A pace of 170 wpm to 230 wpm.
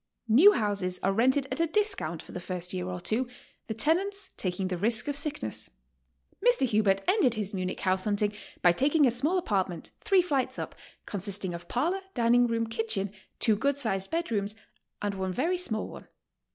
Yes: average, 185 wpm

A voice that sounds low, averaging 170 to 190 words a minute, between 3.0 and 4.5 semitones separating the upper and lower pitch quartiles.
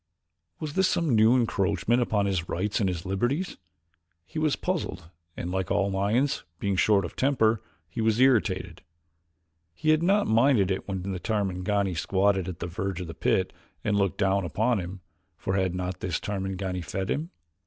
Yes: low, 100 Hz; average, 175 wpm; average, 4.0 semitones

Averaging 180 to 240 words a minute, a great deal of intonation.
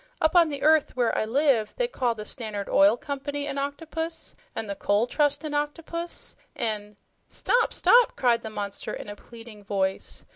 Yes: average, 185 wpm; wide, 6.0 semitones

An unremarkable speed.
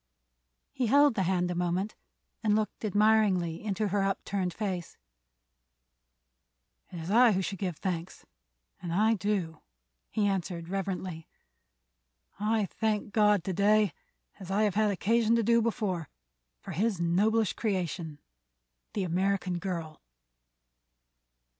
No: slow, 125 wpm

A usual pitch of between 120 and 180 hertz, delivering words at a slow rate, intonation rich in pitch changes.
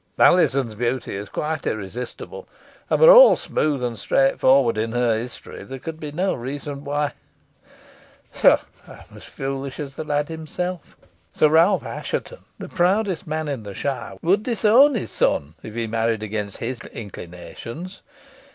No: medium, 140 Hz; average, 155 wpm; wide, 5.9 semitones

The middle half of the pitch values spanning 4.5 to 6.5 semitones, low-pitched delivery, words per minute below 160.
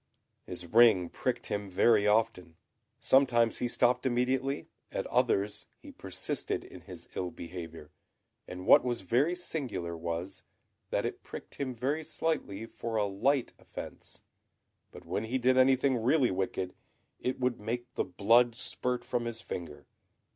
Yes: average, 5.3 semitones; low, 115 Hz; average, 145 wpm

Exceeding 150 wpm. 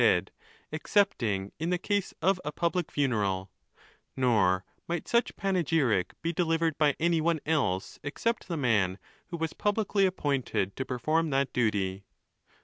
No: average, 145 wpm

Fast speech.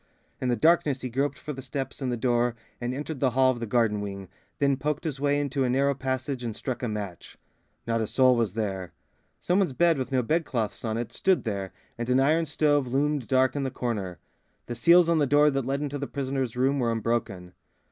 Yes: fast, 230 wpm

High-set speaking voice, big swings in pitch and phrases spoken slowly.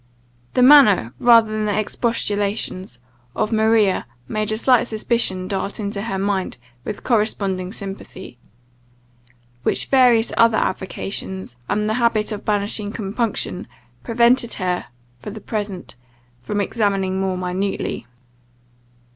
No: high, 210 Hz; average, 2.8 semitones; slow, 120 wpm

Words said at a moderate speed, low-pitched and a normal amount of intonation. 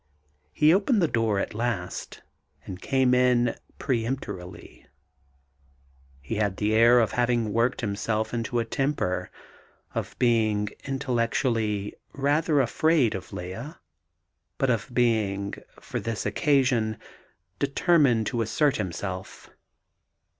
No: slow, 115 wpm; low, 115 Hz; average, 4.0 semitones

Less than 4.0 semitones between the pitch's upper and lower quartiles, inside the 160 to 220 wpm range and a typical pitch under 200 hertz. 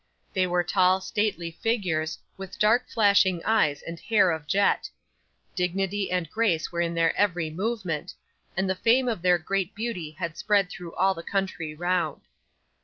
Yes: average, 3.4 semitones; average, 165 wpm; medium, 185 Hz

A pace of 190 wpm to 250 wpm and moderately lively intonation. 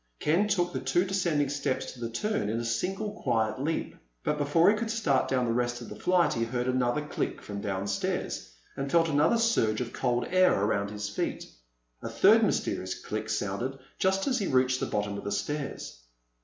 No: average, 200 wpm; wide, 7.7 semitones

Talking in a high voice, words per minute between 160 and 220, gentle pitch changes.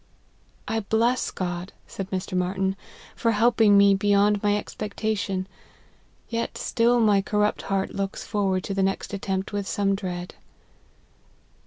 No: high, 200 Hz; average, 150 wpm; narrow, 1.7 semitones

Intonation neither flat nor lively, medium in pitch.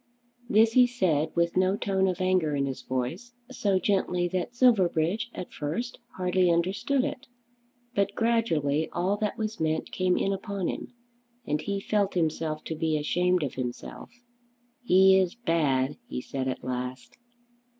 Yes: average, 4.4 semitones; medium, 180 Hz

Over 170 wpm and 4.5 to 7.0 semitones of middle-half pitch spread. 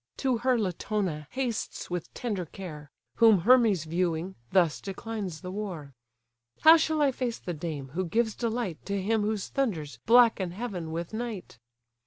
No: average, 155 wpm; wide, 5.4 semitones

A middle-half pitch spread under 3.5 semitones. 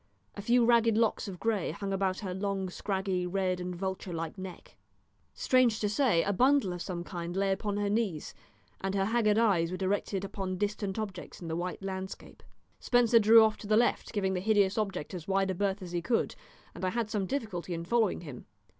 Yes: average, 2.8 semitones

